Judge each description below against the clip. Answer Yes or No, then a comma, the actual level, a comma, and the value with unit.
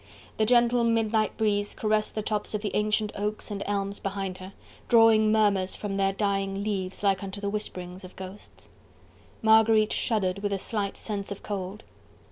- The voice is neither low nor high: No, high, 205 Hz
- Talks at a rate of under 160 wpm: No, average, 170 wpm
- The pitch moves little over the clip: Yes, narrow, 1.6 semitones